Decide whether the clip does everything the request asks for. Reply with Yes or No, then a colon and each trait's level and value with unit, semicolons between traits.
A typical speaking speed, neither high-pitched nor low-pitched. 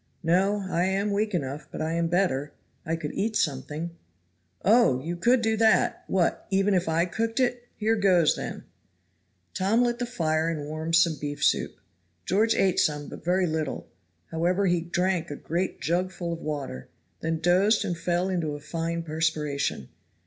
Yes: average, 170 wpm; medium, 170 Hz